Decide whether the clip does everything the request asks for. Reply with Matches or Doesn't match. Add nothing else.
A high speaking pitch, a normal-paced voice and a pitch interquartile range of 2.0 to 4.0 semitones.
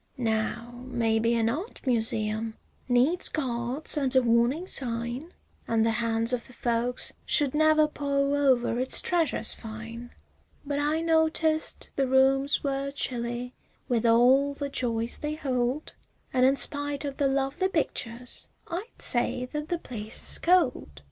Matches